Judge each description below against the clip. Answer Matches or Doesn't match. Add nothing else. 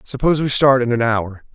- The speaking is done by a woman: Doesn't match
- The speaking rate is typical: Doesn't match